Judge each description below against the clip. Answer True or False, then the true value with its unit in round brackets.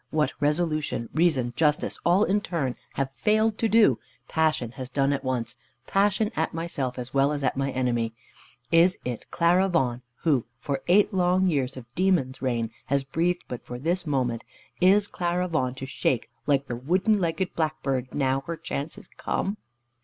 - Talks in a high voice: False (150 Hz)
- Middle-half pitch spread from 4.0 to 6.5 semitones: True (5.5 semitones)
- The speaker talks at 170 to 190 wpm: True (175 wpm)